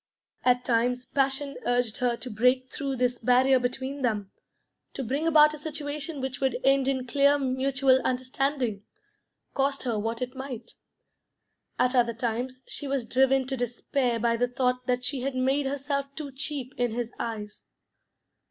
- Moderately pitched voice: No, very high, 255 Hz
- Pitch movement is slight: Yes, narrow, 1.9 semitones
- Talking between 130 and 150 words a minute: No, average, 160 wpm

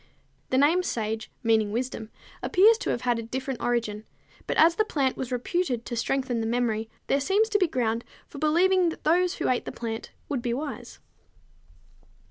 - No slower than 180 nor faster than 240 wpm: Yes, average, 185 wpm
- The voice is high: Yes, very high, 255 Hz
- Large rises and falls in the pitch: Yes, wide, 6.1 semitones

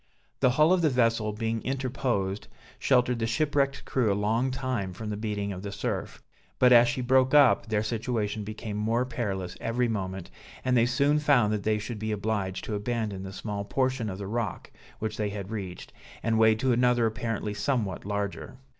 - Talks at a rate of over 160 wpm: Yes, average, 190 wpm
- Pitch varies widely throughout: No, average, 3.3 semitones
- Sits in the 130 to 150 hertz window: No, low, 110 Hz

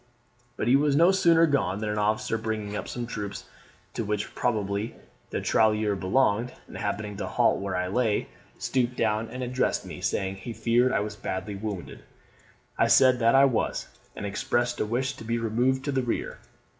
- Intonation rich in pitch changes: No, average, 3.5 semitones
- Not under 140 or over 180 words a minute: No, average, 190 wpm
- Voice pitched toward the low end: Yes, low, 110 Hz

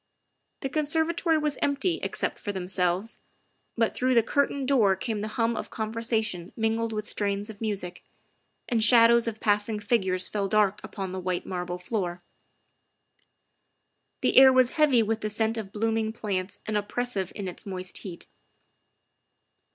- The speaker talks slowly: No, average, 155 wpm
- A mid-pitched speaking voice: No, high, 220 Hz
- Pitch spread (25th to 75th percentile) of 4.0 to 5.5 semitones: No, average, 3.5 semitones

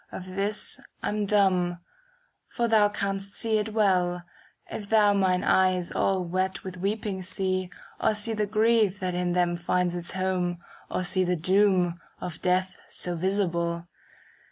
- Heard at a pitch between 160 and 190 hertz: Yes, medium, 185 Hz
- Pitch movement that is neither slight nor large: No, narrow, 2.3 semitones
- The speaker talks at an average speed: Yes, average, 155 wpm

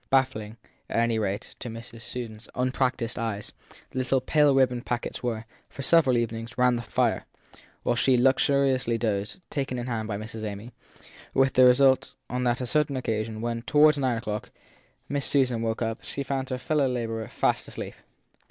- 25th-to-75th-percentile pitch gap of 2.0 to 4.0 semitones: Yes, average, 2.7 semitones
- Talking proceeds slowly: No, average, 185 wpm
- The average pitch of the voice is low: Yes, low, 125 Hz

